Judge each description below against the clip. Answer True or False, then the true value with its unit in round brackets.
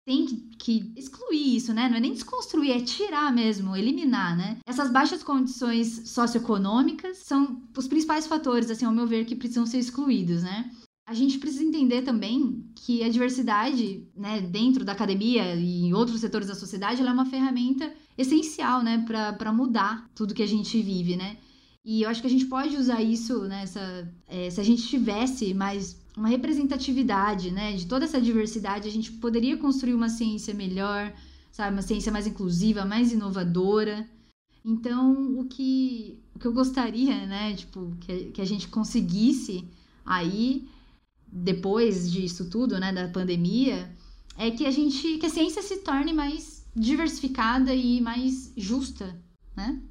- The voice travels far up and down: False (4.1 semitones)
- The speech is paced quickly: False (165 wpm)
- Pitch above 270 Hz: False (235 Hz)